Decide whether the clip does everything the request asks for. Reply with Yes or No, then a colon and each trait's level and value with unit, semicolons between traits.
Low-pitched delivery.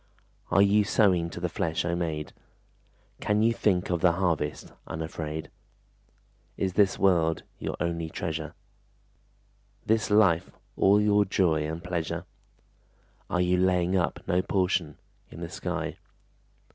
Yes: very low, 90 Hz